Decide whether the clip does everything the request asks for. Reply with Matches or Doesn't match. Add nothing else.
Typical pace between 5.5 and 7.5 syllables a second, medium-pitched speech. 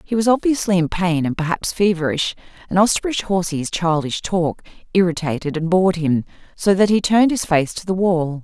Matches